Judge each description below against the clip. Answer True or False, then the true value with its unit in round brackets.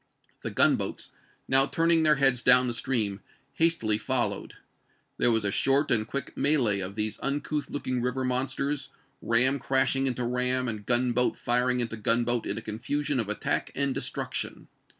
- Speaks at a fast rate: False (165 wpm)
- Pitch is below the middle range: True (125 Hz)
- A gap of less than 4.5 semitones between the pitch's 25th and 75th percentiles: True (2.8 semitones)